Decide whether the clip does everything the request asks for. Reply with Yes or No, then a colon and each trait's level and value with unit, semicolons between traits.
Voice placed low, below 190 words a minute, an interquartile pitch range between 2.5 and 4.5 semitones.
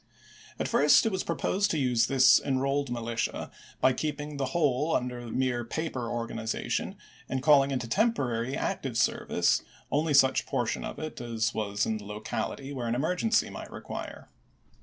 Yes: low, 130 Hz; average, 160 wpm; average, 3.8 semitones